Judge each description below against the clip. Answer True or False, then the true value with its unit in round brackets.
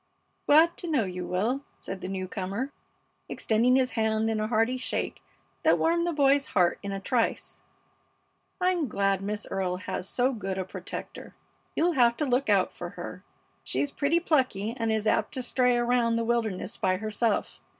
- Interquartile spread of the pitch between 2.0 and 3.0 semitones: False (5.0 semitones)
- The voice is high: True (230 Hz)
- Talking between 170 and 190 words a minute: True (180 wpm)